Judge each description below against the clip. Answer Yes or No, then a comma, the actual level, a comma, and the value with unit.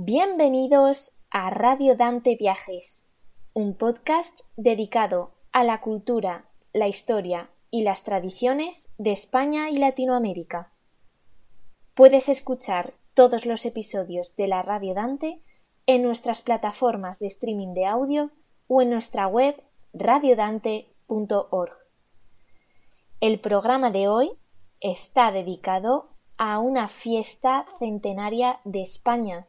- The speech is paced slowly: Yes, slow, 110 wpm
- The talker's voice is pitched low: No, high, 230 Hz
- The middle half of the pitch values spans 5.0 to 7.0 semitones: No, average, 4.3 semitones